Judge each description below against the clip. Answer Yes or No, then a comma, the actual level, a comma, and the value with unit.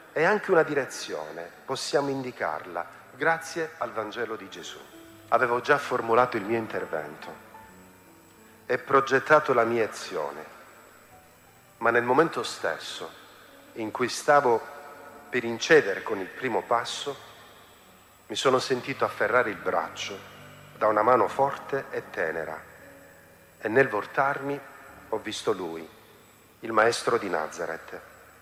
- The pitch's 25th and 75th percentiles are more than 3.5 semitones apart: Yes, average, 4.9 semitones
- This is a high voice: No, low, 120 Hz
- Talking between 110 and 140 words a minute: Yes, average, 120 wpm